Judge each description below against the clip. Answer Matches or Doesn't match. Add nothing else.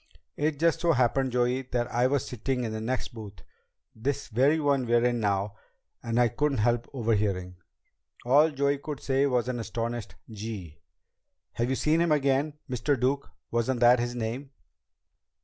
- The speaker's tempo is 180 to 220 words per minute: Doesn't match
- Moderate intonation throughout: Matches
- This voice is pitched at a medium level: Doesn't match